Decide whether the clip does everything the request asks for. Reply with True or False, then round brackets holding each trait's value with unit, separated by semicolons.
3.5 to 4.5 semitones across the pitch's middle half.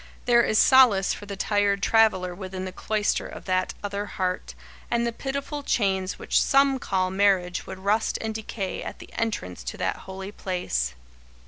False (3.1 semitones)